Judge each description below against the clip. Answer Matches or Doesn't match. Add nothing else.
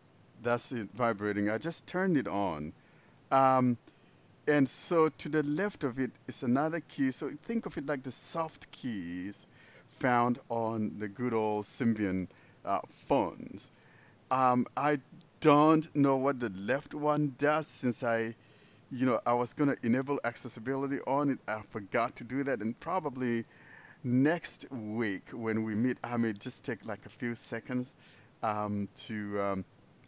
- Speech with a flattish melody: Doesn't match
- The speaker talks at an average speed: Matches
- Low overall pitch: Matches